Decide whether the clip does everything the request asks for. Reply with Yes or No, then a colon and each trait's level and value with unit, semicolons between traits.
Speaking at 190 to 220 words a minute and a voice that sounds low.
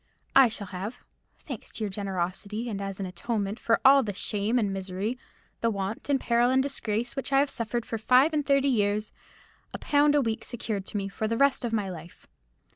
No: average, 200 wpm; high, 225 Hz